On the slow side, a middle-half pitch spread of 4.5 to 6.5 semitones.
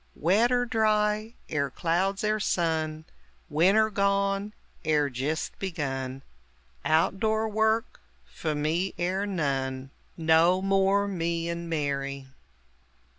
Yes: slow, 110 wpm; average, 4.8 semitones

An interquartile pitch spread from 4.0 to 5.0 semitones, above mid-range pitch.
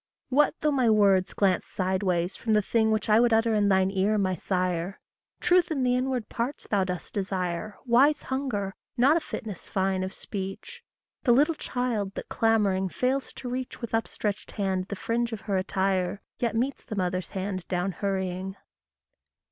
Yes: average, 4.3 semitones; high, 205 Hz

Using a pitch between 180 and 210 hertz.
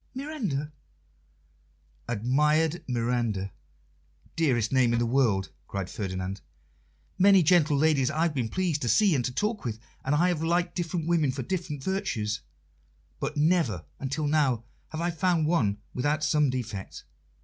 No: medium, 145 Hz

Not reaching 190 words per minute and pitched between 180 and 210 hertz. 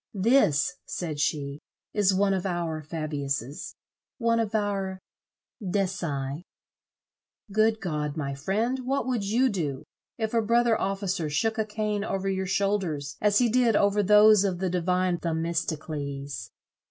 Yes: average, 140 wpm; high, 190 Hz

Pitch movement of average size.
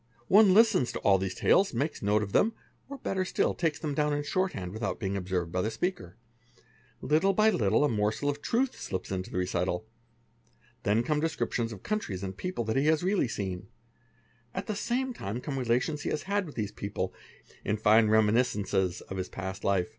No: wide, 8.8 semitones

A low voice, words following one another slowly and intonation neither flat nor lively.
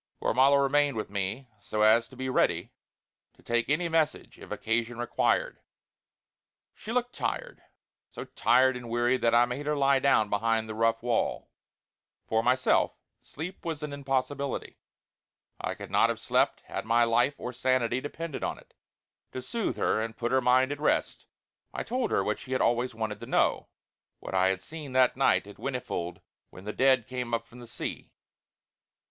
No: low, 125 Hz; average, 180 wpm; average, 3.4 semitones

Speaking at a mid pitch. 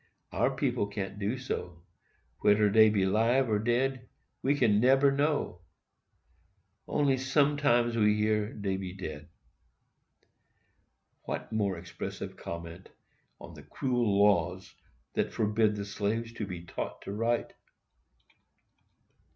No: low, 105 Hz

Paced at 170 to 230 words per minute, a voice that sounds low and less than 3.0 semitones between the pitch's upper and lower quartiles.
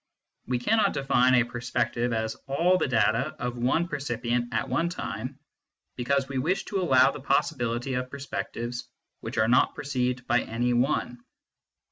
No: average, 155 wpm; low, 125 Hz; narrow, 2.5 semitones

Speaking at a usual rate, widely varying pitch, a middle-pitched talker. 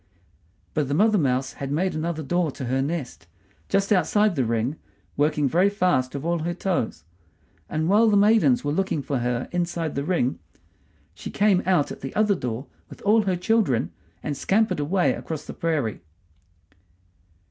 Yes: average, 170 wpm; wide, 5.9 semitones; medium, 165 Hz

